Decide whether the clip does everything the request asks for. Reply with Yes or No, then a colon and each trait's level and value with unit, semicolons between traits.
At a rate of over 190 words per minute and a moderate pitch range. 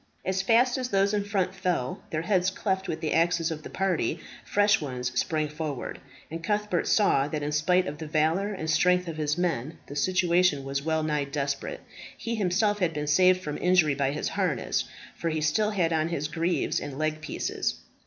Yes: average, 200 wpm; average, 3.8 semitones